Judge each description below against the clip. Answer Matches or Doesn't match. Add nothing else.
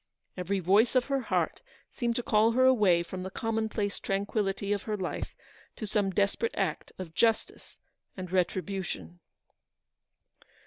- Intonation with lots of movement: Doesn't match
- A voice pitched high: Matches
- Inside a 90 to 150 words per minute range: Matches